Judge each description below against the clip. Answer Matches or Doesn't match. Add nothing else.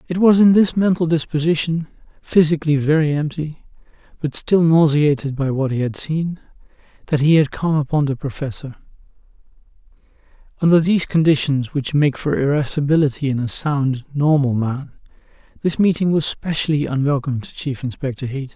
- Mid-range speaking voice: Matches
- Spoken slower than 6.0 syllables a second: Matches